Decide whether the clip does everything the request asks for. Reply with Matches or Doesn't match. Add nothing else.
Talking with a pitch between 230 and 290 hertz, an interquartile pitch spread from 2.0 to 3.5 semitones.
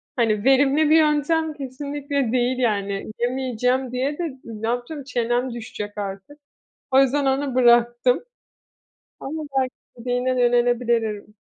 Matches